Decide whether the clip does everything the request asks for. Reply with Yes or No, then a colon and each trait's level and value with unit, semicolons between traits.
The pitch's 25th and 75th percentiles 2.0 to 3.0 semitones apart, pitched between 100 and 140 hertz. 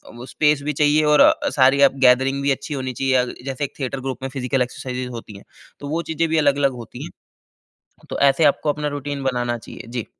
Yes: narrow, 2.5 semitones; low, 135 Hz